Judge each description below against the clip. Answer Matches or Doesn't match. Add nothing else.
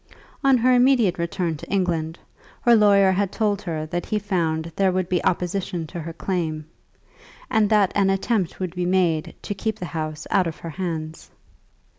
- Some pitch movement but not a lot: Matches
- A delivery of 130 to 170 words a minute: Doesn't match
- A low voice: Doesn't match